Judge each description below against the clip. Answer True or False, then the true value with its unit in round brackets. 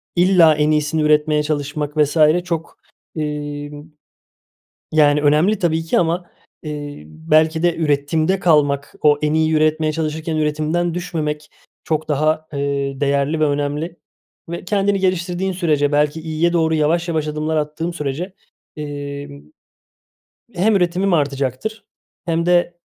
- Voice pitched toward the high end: False (155 Hz)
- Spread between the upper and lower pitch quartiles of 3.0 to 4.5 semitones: False (2.5 semitones)